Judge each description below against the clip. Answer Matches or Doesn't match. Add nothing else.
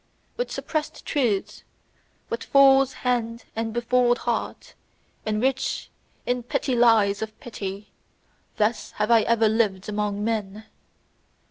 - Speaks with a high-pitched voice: Matches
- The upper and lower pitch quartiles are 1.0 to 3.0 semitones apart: Matches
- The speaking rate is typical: Doesn't match